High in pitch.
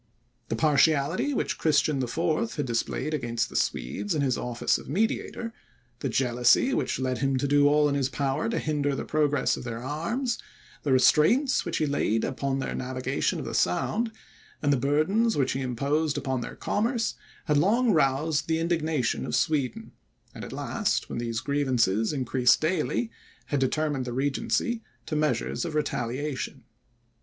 No: medium, 145 Hz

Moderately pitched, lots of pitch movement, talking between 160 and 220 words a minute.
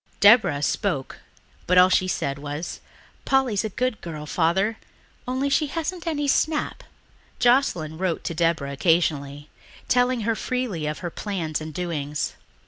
No: medium, 180 Hz; wide, 8.2 semitones; average, 140 wpm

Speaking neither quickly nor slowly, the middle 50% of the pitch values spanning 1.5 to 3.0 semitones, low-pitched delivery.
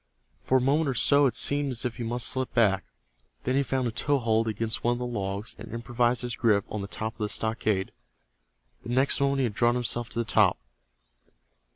No: fast, 225 wpm; average, 2.7 semitones; low, 120 Hz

